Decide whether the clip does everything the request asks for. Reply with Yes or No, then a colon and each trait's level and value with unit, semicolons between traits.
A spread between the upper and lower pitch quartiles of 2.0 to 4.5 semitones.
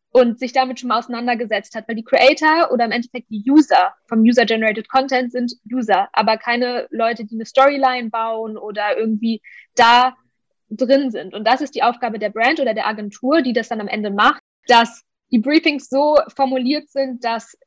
Yes: average, 2.7 semitones